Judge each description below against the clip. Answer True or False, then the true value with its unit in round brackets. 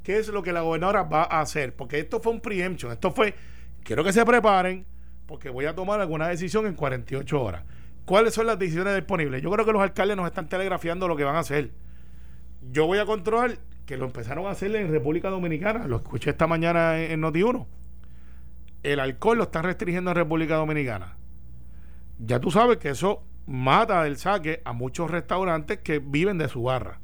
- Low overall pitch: False (160 Hz)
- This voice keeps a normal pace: False (195 wpm)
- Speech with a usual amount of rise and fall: False (6.9 semitones)